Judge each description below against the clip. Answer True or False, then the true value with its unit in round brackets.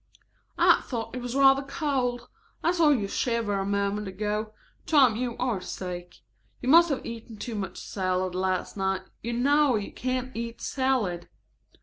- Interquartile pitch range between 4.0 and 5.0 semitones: True (4.7 semitones)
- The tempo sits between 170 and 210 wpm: False (160 wpm)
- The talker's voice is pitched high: True (230 Hz)